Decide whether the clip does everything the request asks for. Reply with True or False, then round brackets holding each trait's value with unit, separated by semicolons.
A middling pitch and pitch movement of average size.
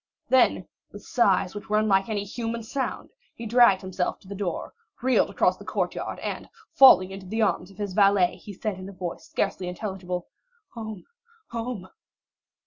False (205 Hz; 3.4 semitones)